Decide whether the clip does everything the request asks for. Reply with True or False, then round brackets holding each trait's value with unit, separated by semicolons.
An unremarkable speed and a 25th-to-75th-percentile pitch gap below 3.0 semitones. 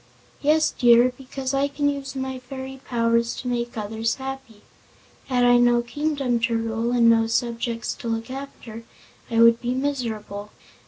True (160 wpm; 2.5 semitones)